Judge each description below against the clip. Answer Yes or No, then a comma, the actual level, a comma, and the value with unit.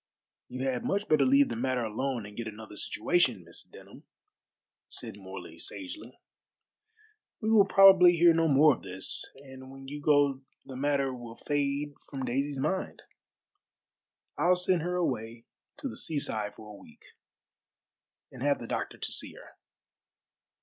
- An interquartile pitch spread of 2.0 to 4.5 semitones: No, average, 5.2 semitones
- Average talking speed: Yes, average, 155 wpm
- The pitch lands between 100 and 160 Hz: Yes, low, 135 Hz